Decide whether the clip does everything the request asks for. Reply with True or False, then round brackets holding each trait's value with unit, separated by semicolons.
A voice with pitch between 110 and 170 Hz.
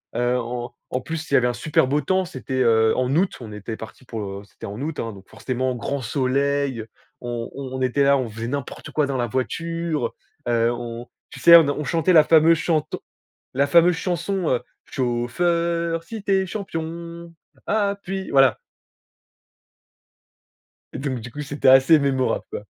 True (140 Hz)